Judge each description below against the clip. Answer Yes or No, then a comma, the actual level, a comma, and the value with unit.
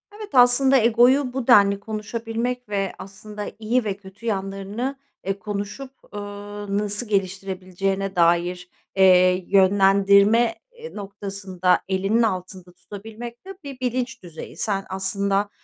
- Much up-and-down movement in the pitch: No, average, 3.1 semitones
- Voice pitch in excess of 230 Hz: No, high, 205 Hz